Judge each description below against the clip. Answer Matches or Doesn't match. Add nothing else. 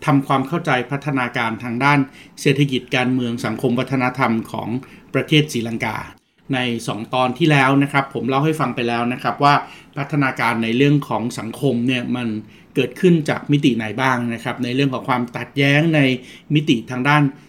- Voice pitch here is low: Matches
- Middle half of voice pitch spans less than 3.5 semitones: Matches